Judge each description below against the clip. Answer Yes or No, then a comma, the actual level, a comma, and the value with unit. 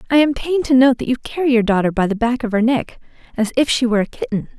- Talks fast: Yes, fast, 290 wpm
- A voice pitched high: Yes, very high, 250 Hz